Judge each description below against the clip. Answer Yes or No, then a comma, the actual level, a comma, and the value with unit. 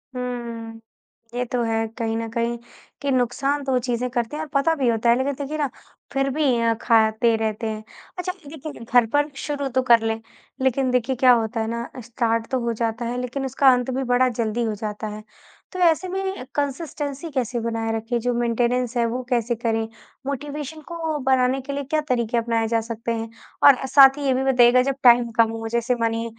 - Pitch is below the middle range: No, high, 245 Hz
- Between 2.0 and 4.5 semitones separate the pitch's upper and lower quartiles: Yes, average, 3.0 semitones